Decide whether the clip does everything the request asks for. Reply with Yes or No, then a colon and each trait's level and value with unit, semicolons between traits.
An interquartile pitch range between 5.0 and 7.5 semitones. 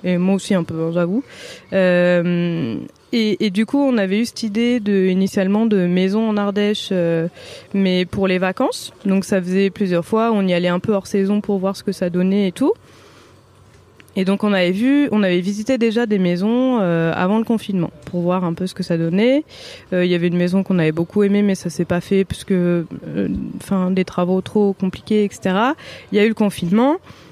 No: average, 3.0 semitones